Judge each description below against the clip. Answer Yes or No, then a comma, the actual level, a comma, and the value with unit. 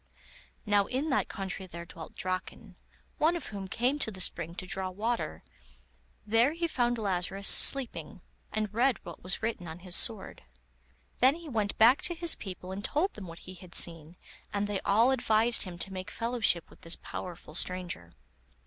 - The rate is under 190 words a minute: Yes, average, 180 wpm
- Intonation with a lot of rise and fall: No, average, 4.8 semitones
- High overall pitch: Yes, high, 200 Hz